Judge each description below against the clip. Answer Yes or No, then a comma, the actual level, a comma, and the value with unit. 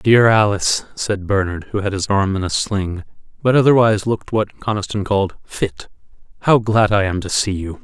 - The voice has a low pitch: Yes, low, 100 Hz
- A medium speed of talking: Yes, average, 190 wpm